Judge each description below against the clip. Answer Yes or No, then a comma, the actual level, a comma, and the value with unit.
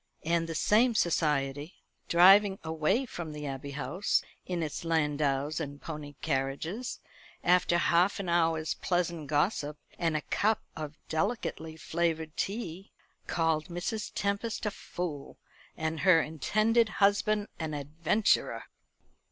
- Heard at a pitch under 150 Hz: No, medium, 165 Hz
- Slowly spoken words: Yes, slow, 125 wpm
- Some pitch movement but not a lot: Yes, average, 4.3 semitones